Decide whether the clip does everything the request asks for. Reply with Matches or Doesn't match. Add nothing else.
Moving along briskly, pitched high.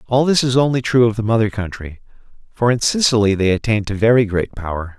Doesn't match